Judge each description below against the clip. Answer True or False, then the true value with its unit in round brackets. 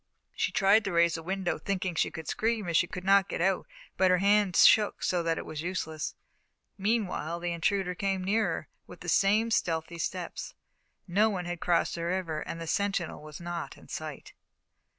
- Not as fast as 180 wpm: False (195 wpm)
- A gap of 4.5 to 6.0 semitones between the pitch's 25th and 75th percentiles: False (2.8 semitones)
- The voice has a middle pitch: True (180 Hz)